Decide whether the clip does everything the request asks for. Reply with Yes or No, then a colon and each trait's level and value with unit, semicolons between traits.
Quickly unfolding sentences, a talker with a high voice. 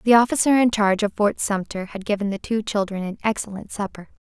Yes: fast, 210 wpm; high, 210 Hz